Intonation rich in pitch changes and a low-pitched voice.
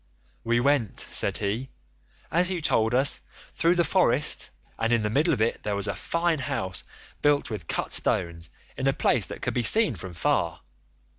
Yes: wide, 6.4 semitones; low, 120 Hz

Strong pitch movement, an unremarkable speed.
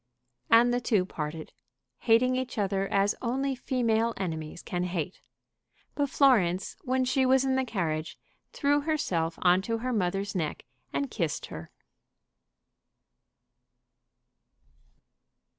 No: wide, 6.3 semitones; slow, 120 wpm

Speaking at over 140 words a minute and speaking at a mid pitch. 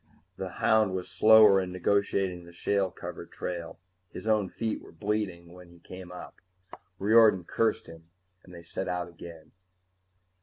No: average, 160 wpm; very low, 95 Hz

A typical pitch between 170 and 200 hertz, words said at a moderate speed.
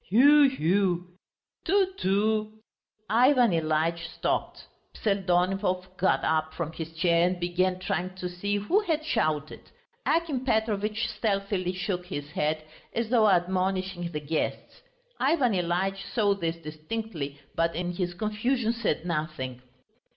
No: medium, 185 Hz; slow, 130 wpm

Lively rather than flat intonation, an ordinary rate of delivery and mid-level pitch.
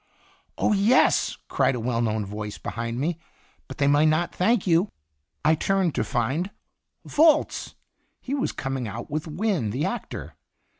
Yes: wide, 8.3 semitones; average, 155 wpm; medium, 155 Hz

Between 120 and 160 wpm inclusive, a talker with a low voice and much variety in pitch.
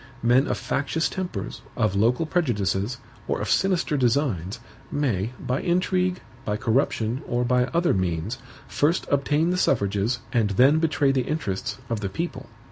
Yes: average, 150 wpm; low, 125 Hz; wide, 6.5 semitones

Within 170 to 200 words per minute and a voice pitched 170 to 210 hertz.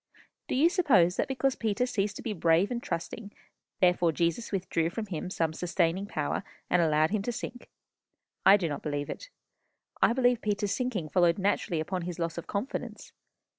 Yes: average, 180 wpm; high, 190 Hz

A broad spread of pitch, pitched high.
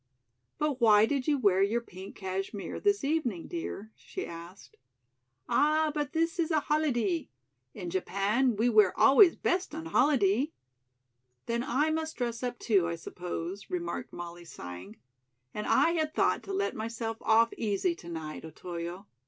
Yes: wide, 8.3 semitones; high, 230 Hz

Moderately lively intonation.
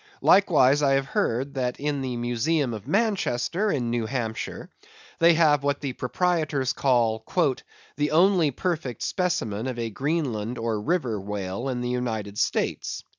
Yes: average, 4.8 semitones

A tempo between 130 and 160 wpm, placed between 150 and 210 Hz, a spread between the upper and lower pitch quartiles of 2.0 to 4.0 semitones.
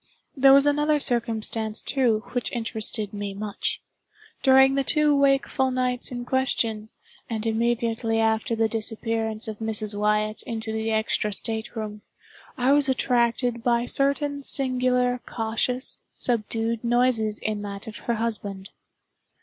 No: slow, 135 wpm; high, 230 Hz; average, 2.7 semitones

